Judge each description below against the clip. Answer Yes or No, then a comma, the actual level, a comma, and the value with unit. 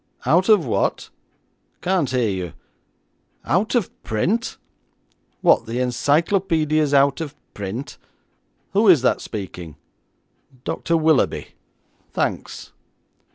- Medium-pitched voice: Yes, medium, 145 Hz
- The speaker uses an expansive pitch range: Yes, wide, 6.6 semitones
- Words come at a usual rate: No, slow, 100 wpm